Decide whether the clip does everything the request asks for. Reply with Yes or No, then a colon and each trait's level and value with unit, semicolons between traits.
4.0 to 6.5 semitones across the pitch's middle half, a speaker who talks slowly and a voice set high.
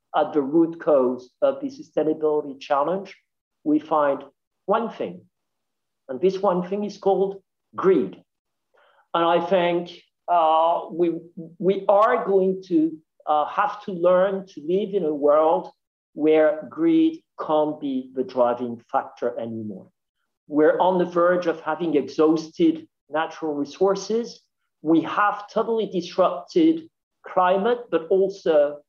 No: average, 4.4 semitones; slow, 125 wpm; medium, 175 Hz